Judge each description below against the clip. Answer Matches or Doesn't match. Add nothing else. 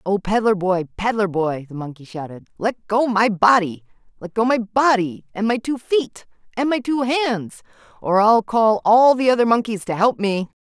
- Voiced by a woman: Matches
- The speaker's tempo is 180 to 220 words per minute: Matches